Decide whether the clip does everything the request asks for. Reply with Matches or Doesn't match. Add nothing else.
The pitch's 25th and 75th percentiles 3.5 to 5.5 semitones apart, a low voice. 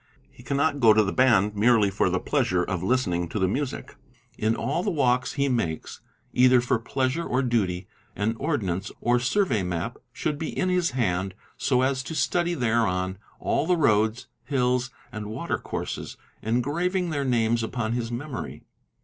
Matches